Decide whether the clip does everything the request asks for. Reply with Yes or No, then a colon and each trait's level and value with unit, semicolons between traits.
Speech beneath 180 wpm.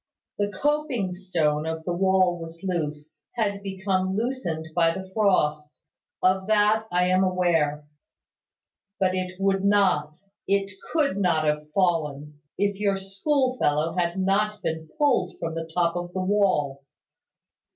Yes: average, 140 wpm